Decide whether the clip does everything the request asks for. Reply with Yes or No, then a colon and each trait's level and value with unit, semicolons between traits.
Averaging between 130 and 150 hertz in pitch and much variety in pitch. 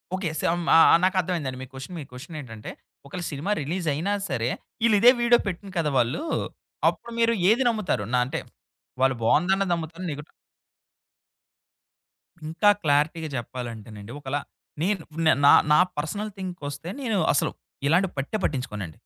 No: medium, 160 Hz; wide, 6.1 semitones